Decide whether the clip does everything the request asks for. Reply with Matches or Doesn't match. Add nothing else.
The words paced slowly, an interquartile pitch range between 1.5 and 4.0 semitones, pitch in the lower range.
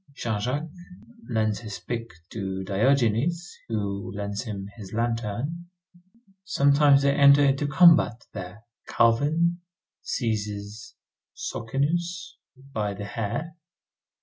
Doesn't match